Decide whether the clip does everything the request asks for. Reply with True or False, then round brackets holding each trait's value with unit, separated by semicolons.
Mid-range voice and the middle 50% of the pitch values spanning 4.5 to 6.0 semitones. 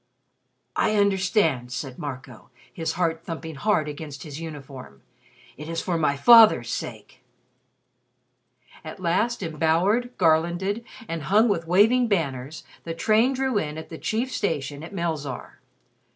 True (165 Hz; 5.4 semitones)